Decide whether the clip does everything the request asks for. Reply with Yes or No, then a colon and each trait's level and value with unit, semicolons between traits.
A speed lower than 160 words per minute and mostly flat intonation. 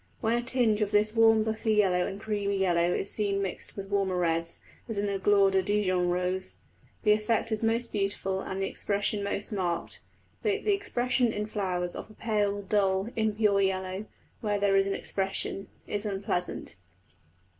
No: average, 175 wpm; narrow, 2.0 semitones